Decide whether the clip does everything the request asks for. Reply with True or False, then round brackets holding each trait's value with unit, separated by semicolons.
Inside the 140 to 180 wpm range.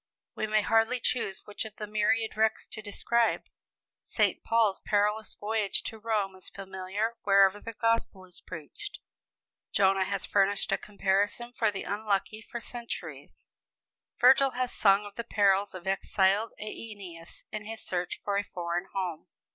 True (155 wpm)